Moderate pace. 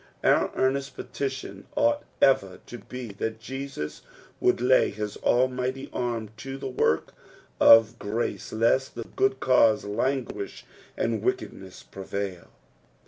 No: slow, 125 wpm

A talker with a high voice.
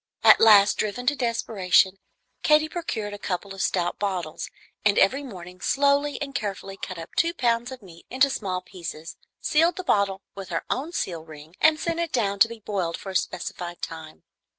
Yes: high, 200 Hz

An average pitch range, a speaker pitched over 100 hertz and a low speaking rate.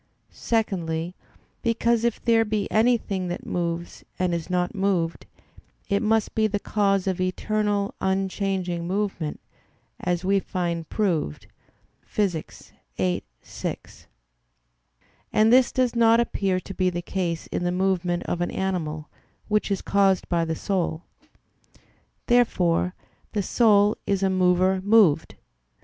Yes: average, 3.2 semitones; high, 190 Hz; slow, 130 wpm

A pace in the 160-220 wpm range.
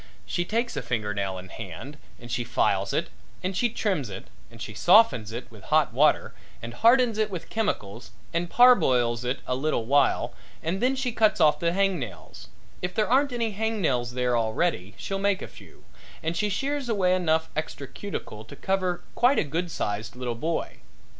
Yes: average, 190 wpm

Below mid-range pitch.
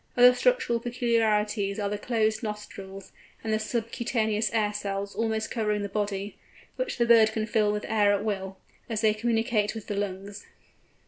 No: high, 215 Hz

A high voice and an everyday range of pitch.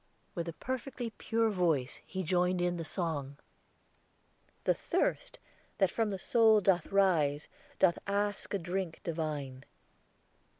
No: medium, 180 Hz; average, 4.0 semitones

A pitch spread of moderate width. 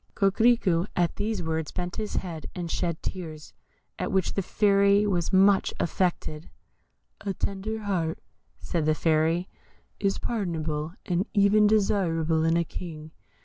Yes: average, 3.5 semitones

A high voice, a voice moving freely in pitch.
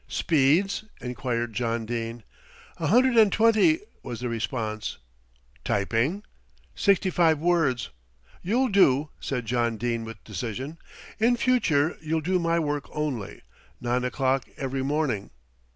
No: low, 135 Hz; wide, 6.7 semitones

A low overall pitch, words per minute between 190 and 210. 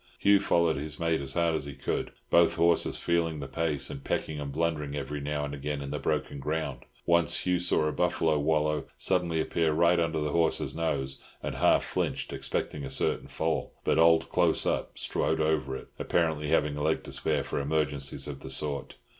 Yes: very low, 75 Hz; average, 200 wpm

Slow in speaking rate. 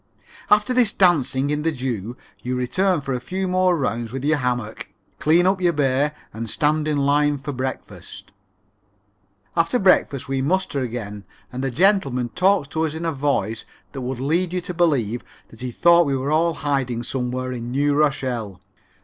No: average, 185 wpm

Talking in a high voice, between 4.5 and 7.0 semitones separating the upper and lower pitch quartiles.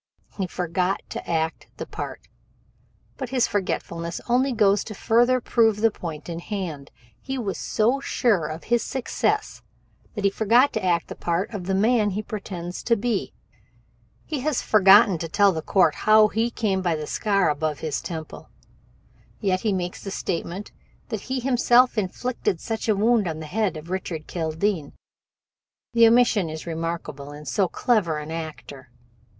Yes: high, 195 Hz; average, 5.2 semitones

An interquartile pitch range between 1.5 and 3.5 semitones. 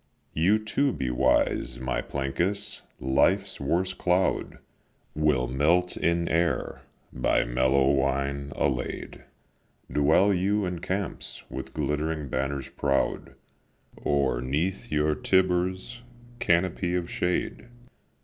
No: average, 5.3 semitones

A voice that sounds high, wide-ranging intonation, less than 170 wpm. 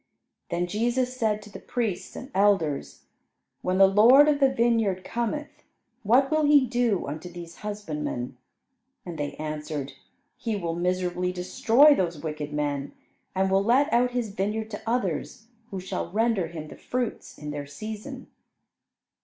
Yes: high, 200 Hz; wide, 5.9 semitones; average, 155 wpm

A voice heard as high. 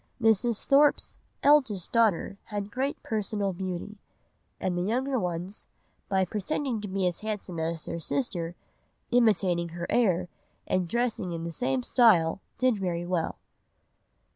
Yes: high, 195 Hz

